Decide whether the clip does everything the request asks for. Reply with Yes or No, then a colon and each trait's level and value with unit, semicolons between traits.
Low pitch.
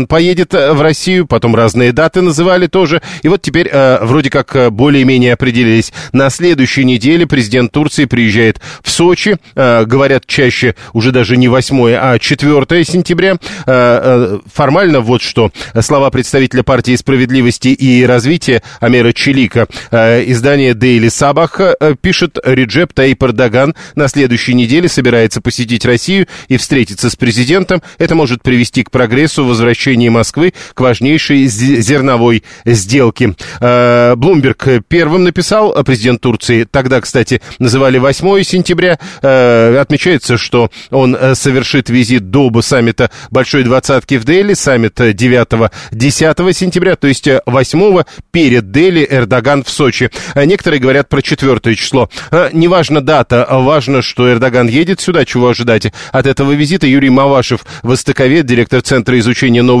Yes: low, 130 Hz